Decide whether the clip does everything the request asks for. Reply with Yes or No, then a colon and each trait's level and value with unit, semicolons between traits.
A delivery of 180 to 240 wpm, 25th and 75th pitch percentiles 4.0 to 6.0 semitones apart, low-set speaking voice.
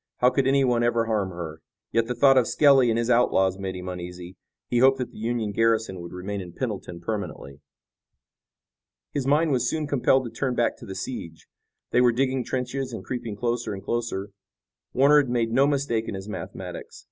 Yes: average, 195 wpm; average, 4.9 semitones; low, 115 Hz